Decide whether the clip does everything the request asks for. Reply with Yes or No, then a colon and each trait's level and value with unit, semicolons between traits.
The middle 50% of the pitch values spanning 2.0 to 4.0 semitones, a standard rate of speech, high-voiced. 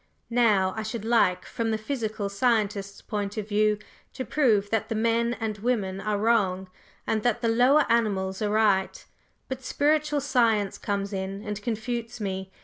Yes: average, 2.8 semitones; average, 165 wpm; high, 215 Hz